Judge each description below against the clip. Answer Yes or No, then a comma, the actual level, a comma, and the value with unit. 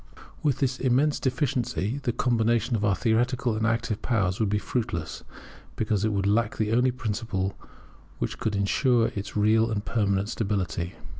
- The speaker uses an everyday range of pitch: Yes, average, 3.0 semitones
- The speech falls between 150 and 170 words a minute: Yes, average, 160 wpm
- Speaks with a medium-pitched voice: No, low, 110 Hz